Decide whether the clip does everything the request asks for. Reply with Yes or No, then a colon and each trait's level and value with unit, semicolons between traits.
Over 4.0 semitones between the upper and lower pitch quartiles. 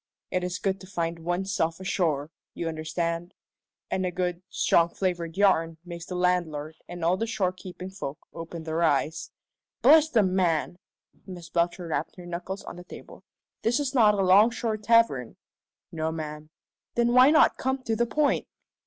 No: average, 3.2 semitones